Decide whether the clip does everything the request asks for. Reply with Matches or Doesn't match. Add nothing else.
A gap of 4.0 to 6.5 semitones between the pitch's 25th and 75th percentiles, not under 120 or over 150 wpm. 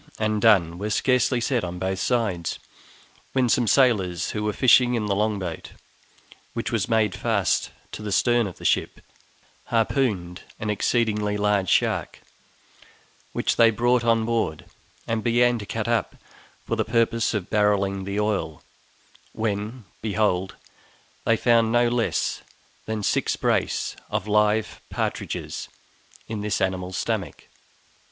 Doesn't match